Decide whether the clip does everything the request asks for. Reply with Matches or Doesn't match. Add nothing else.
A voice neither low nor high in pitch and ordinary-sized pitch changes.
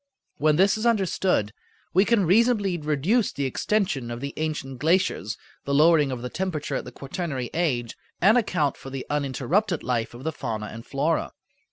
Doesn't match